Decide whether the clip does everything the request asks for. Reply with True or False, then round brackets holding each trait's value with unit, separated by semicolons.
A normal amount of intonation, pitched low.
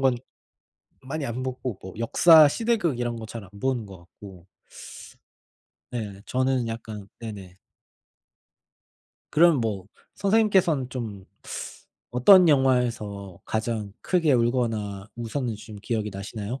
True (4.3 semitones; 120 Hz)